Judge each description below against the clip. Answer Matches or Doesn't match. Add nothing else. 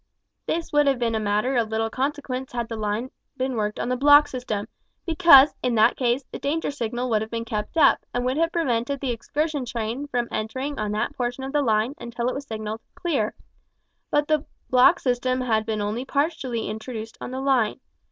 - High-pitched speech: Matches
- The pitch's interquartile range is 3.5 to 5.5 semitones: Matches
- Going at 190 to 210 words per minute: Matches